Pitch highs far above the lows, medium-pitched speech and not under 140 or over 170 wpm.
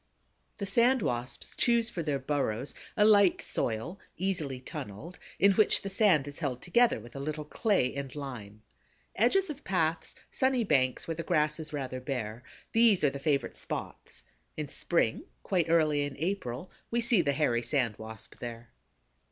Yes: wide, 7.0 semitones; medium, 150 Hz; average, 165 wpm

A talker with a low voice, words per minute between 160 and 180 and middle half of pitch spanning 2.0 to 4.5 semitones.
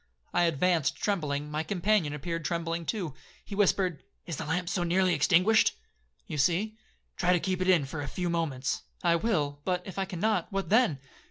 No: medium, 175 Hz; average, 170 wpm; average, 3.7 semitones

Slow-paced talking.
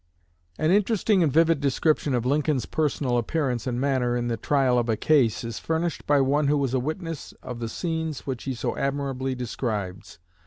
No: average, 190 wpm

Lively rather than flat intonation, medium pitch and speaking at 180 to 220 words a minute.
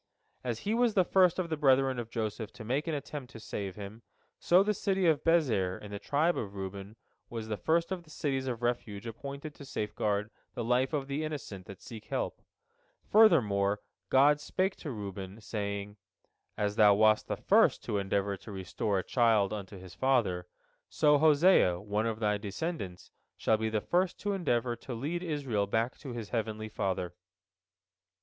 No: wide, 6.4 semitones; low, 115 Hz; average, 185 wpm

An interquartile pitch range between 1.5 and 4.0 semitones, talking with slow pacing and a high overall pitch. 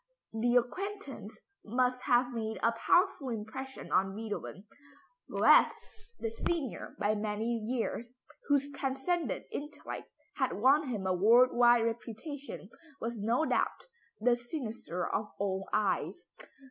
Yes: average, 3.6 semitones; slow, 120 wpm; high, 240 Hz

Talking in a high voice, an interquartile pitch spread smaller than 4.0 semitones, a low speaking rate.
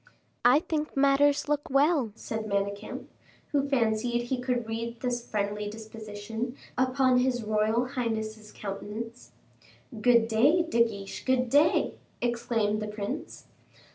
Yes: high, 235 Hz; average, 3.2 semitones; slow, 125 wpm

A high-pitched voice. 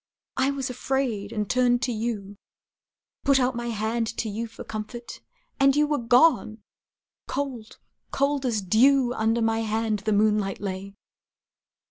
Yes: high, 230 Hz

